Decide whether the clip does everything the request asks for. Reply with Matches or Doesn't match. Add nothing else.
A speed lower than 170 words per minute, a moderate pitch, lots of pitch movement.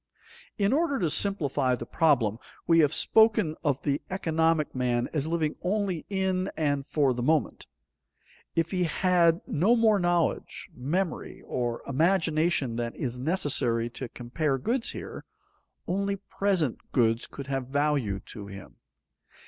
Matches